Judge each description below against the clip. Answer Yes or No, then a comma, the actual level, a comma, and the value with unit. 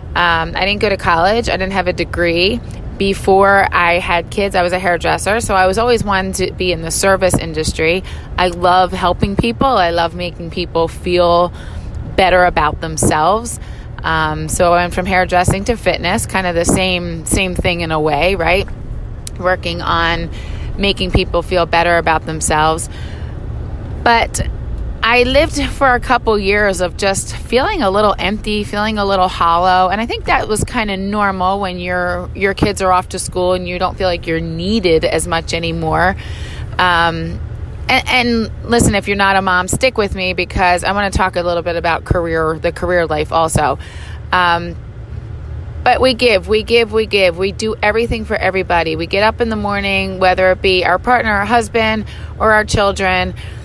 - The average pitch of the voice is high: No, medium, 180 Hz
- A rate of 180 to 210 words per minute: Yes, average, 185 wpm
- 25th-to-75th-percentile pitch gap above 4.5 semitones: No, average, 2.8 semitones